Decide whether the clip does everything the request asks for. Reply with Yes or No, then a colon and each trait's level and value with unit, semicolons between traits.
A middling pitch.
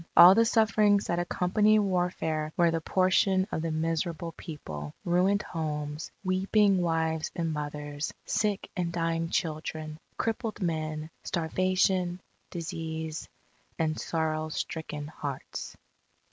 Yes: medium, 165 Hz